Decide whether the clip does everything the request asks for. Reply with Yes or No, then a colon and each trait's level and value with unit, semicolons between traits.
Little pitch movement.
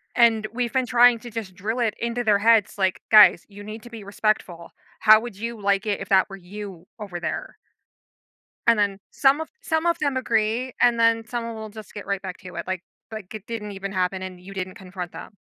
No: average, 3.1 semitones